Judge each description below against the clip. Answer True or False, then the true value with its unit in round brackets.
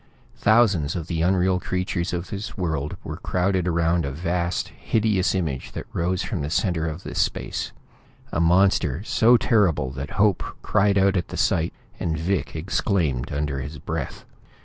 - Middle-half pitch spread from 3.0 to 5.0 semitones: True (3.5 semitones)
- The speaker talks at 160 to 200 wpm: True (165 wpm)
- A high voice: False (90 Hz)